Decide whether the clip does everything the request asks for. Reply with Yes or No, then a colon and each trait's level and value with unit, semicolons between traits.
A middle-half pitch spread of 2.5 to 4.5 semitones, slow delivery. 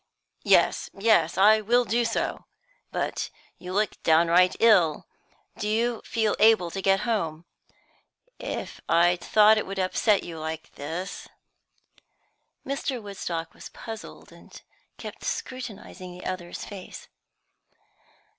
Yes: average, 4.1 semitones; slow, 125 wpm